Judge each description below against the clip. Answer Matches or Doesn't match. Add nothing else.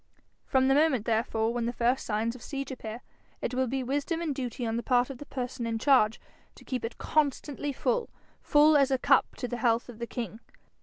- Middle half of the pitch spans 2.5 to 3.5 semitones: Matches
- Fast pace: Matches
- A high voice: Matches